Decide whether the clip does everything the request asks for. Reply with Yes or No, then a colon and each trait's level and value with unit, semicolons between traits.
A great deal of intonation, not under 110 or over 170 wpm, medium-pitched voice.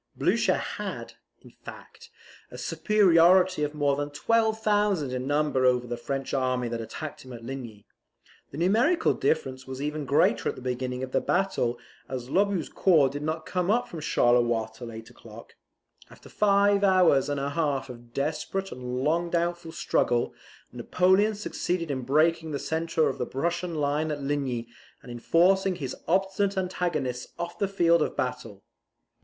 Yes: wide, 6.0 semitones; average, 165 wpm; medium, 150 Hz